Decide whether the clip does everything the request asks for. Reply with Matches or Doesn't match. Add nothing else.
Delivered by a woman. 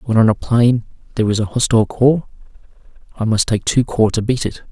Doesn't match